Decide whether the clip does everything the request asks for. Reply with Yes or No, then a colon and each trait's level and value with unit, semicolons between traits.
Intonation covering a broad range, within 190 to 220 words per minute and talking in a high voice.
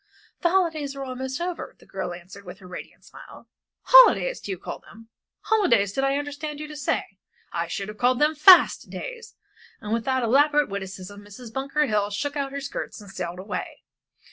Yes: wide, 6.7 semitones; average, 195 wpm; very high, 260 Hz